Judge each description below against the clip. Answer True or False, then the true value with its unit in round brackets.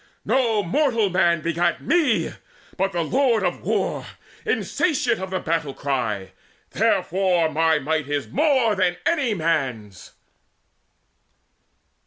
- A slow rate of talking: True (115 wpm)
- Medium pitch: True (175 Hz)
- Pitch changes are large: True (6.5 semitones)